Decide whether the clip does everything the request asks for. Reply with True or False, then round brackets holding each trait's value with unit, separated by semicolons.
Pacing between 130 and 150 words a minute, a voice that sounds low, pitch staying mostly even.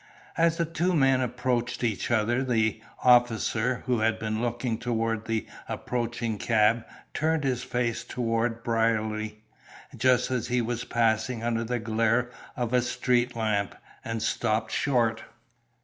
True (140 wpm; 120 Hz; 1.8 semitones)